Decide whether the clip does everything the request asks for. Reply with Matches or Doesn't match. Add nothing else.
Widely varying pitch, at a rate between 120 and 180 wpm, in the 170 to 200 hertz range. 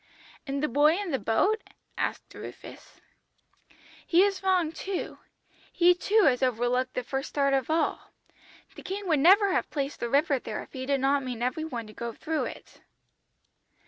Doesn't match